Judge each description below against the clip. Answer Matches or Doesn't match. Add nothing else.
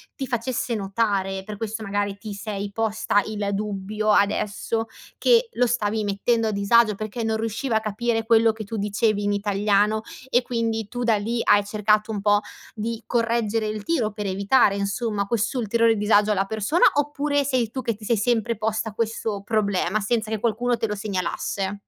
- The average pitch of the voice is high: Matches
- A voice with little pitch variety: Matches